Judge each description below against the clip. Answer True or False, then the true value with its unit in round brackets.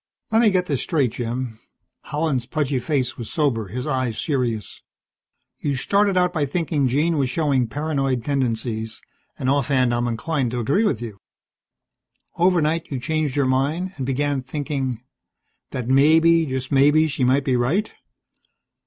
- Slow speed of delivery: False (155 wpm)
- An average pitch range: True (3.9 semitones)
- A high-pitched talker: False (135 Hz)